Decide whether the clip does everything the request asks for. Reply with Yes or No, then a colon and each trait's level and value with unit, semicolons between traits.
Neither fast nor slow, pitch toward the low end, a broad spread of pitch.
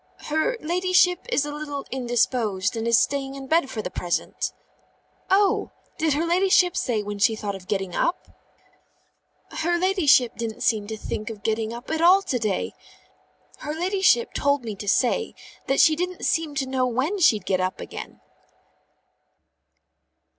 No: average, 160 wpm; very high, 270 Hz; wide, 7.4 semitones